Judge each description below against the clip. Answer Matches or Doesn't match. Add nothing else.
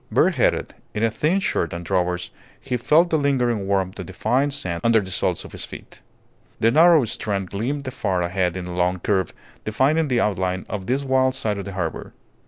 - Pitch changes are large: Matches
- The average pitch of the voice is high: Doesn't match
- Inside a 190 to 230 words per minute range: Matches